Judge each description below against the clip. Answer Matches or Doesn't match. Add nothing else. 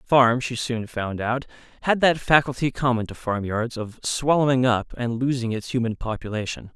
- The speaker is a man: Matches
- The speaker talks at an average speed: Matches